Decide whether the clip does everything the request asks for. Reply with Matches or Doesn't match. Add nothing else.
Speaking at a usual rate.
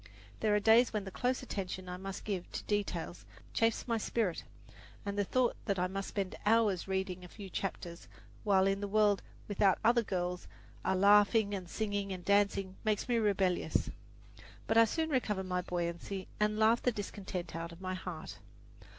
Matches